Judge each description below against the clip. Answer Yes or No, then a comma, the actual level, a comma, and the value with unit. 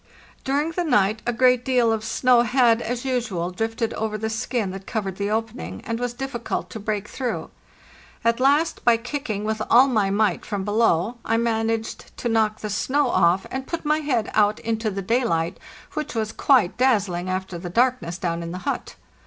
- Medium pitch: No, high, 225 Hz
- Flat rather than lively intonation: No, average, 3.5 semitones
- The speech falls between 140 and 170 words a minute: No, average, 190 wpm